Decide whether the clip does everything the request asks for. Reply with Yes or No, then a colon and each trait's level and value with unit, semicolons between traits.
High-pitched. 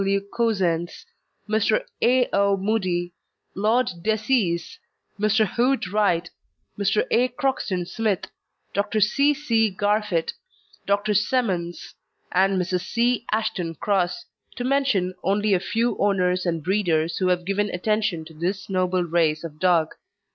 Yes: high, 200 Hz